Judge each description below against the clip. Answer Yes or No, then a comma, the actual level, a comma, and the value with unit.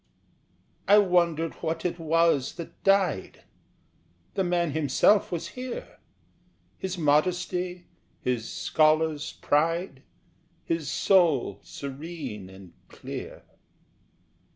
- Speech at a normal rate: No, slow, 90 wpm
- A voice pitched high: No, medium, 165 Hz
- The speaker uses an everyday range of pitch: Yes, average, 3.6 semitones